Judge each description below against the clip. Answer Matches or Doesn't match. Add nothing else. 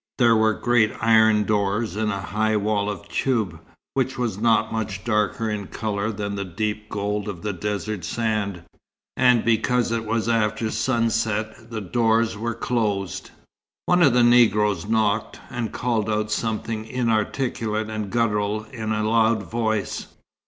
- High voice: Doesn't match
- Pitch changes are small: Matches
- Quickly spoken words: Doesn't match